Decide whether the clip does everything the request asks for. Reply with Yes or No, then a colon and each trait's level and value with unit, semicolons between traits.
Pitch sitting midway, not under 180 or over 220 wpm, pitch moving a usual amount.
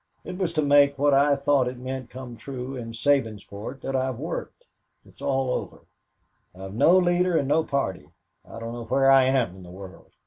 No: low, 130 Hz; average, 200 wpm; average, 3.5 semitones